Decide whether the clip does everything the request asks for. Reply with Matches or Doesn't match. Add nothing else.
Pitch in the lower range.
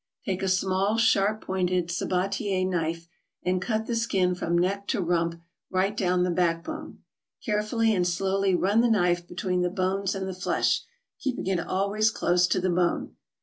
Doesn't match